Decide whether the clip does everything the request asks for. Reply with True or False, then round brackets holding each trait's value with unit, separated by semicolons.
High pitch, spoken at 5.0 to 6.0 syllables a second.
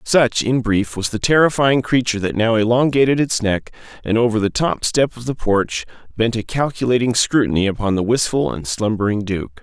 False (115 Hz; 5.3 syllables/s)